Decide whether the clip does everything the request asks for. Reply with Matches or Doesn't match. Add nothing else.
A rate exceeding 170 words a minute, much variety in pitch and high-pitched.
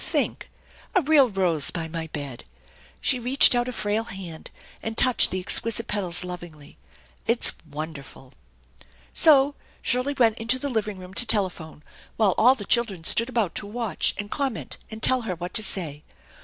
Matches